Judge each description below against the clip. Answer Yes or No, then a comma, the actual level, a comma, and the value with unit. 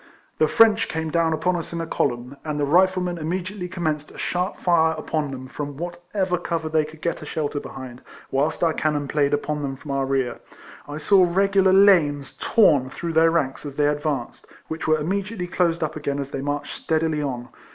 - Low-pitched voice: No, medium, 155 Hz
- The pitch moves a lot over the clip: No, average, 3.4 semitones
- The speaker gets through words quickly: Yes, fast, 210 wpm